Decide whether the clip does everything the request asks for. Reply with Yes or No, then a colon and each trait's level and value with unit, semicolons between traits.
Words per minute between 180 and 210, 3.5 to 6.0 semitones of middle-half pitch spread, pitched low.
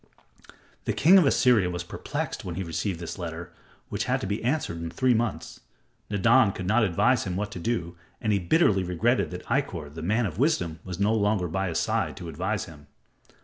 Yes: fast, 205 wpm; average, 5.1 semitones; very low, 95 Hz